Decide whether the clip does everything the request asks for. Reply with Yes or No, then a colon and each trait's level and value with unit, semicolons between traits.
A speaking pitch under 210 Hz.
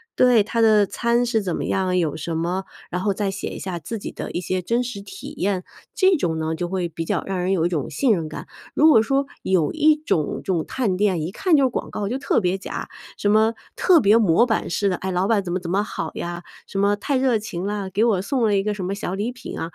Yes: high, 200 Hz